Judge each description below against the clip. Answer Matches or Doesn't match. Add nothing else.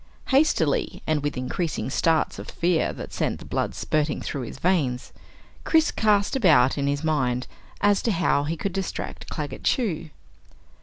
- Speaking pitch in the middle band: Matches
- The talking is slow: Doesn't match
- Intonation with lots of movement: Matches